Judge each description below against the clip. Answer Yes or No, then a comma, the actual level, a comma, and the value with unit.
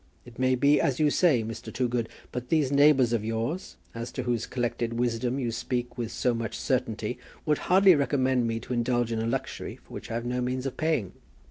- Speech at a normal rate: No, fast, 215 wpm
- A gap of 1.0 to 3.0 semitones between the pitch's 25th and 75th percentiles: Yes, narrow, 2.4 semitones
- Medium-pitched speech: No, low, 125 Hz